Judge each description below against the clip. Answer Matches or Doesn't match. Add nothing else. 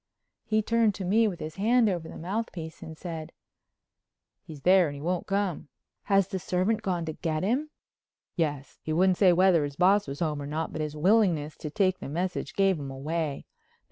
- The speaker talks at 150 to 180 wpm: Doesn't match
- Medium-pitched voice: Matches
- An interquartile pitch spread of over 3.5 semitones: Matches